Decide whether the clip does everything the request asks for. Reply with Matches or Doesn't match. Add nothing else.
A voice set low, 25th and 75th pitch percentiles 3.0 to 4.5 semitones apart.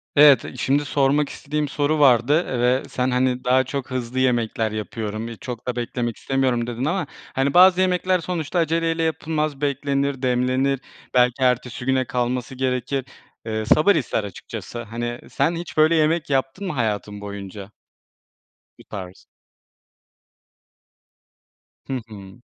Matches